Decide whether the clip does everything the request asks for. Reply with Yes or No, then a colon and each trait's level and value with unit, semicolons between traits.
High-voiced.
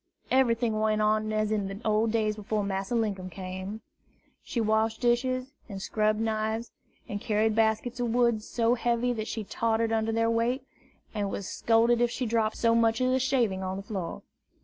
Yes: high, 220 Hz